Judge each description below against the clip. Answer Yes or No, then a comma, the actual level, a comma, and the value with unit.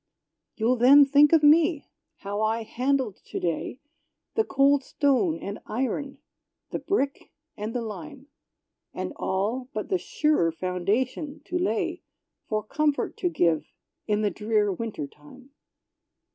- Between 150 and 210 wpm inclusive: No, slow, 135 wpm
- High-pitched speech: Yes, very high, 255 Hz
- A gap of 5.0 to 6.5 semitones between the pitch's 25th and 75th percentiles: Yes, wide, 5.5 semitones